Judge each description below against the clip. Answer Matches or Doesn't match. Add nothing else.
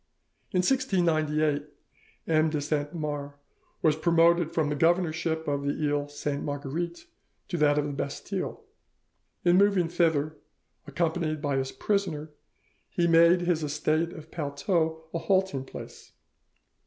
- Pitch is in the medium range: Matches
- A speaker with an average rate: Doesn't match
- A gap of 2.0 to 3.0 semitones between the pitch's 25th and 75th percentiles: Matches